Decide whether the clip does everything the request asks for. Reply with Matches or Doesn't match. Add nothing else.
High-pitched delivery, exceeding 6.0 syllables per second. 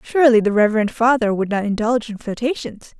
Matches